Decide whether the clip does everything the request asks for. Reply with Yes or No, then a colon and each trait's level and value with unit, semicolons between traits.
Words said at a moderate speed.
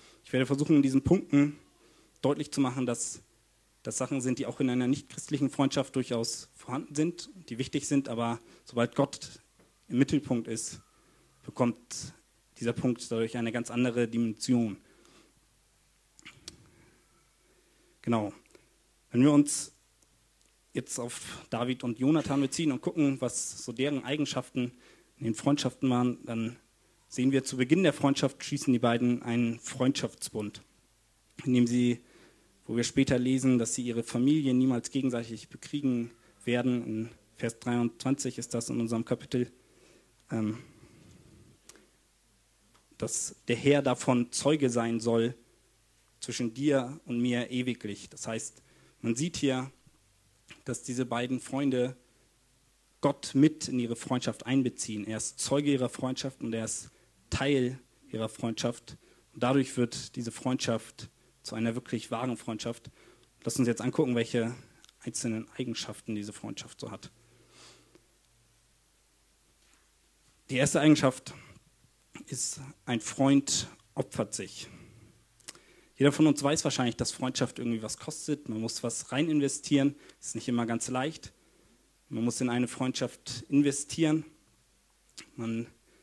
Yes: average, 135 wpm